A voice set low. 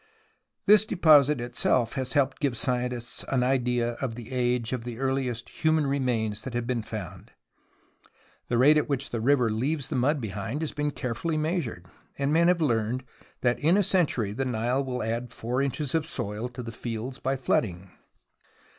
Yes: low, 125 Hz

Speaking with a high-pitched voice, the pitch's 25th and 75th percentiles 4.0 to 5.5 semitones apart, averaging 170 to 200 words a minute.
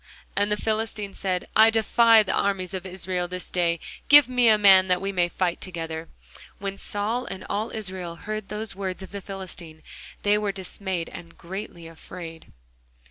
No: high, 195 Hz; average, 2.8 semitones; average, 175 wpm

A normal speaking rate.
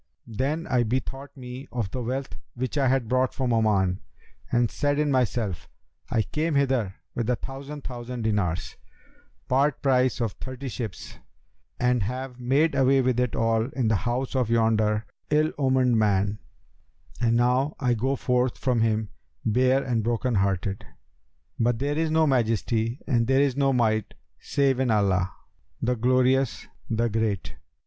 Yes: average, 155 wpm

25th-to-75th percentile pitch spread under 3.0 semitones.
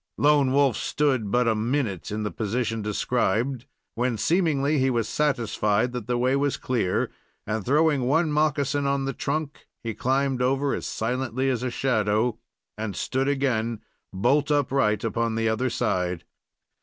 No: average, 3.8 semitones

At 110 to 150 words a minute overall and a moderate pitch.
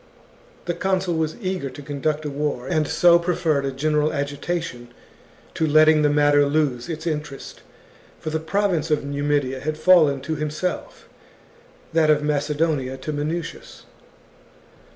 Yes: average, 140 wpm; medium, 150 Hz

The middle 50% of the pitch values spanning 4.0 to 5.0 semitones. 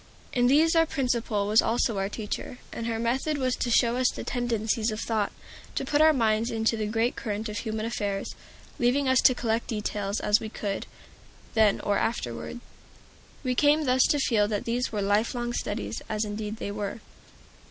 No: average, 2.9 semitones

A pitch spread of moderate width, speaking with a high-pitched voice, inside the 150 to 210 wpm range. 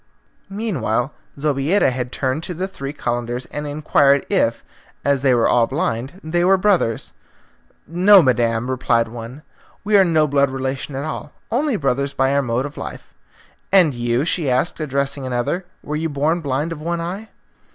No: average, 4.7 semitones; medium, 140 Hz; average, 170 wpm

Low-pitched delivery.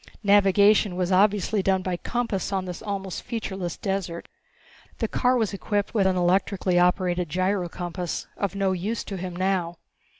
No: high, 190 Hz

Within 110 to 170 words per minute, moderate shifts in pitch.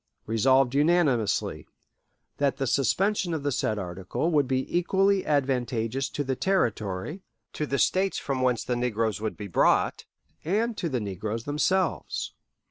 No: average, 145 wpm; wide, 6.3 semitones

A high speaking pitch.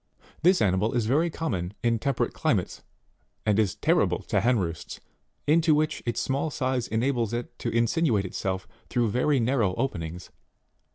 No: low, 120 Hz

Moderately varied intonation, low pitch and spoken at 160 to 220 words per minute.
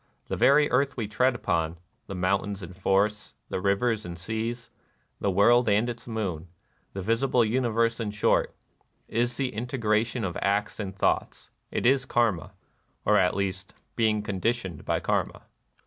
Yes: average, 3.4 semitones; low, 110 Hz; average, 165 wpm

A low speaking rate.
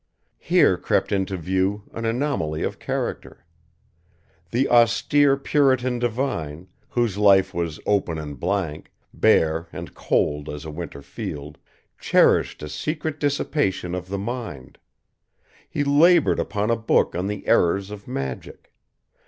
Yes: slow, 130 wpm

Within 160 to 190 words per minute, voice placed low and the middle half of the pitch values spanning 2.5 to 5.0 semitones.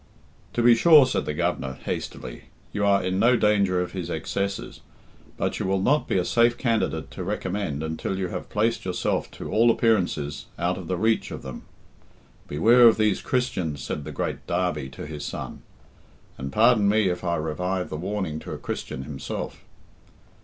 No: average, 180 wpm; very low, 95 Hz; wide, 5.5 semitones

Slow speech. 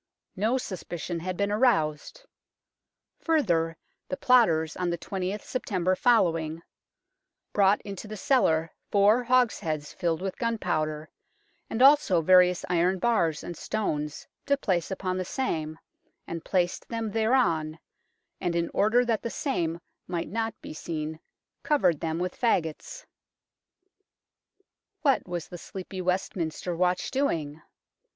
Yes: slow, 130 wpm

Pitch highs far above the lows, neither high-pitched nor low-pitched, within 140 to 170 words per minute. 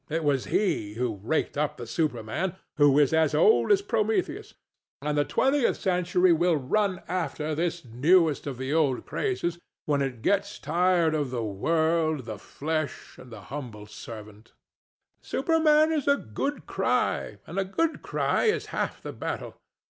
Yes: wide, 6.4 semitones; medium, 160 Hz; average, 165 wpm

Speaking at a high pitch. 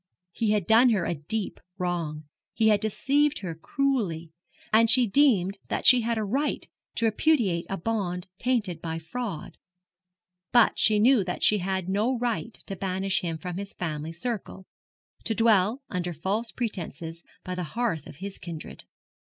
Yes: high, 200 Hz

